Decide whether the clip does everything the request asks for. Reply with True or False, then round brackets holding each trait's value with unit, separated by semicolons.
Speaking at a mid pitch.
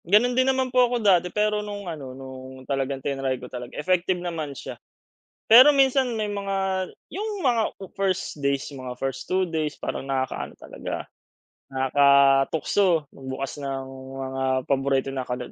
True (155 Hz)